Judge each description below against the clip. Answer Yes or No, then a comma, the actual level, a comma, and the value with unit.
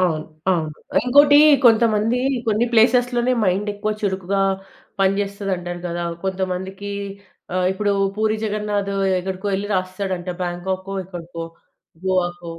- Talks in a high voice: Yes, high, 195 Hz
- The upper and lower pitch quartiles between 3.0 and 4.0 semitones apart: No, narrow, 2.6 semitones